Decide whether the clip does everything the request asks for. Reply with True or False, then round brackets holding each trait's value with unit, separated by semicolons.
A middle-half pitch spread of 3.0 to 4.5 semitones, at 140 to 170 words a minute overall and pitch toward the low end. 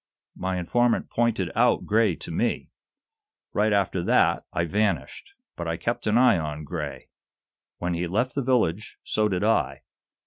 False (4.9 semitones; 160 wpm; 100 Hz)